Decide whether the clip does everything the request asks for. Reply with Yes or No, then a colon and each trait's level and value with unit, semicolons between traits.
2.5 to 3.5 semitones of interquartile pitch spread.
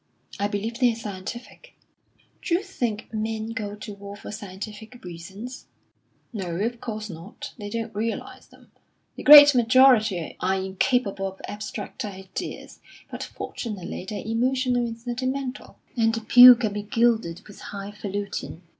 Yes: average, 3.1 semitones